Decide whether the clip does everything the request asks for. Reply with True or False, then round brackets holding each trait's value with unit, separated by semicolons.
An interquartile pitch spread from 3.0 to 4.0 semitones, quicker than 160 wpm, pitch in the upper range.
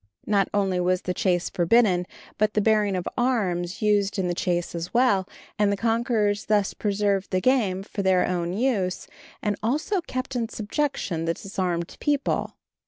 True (3.5 semitones; 170 wpm; 200 Hz)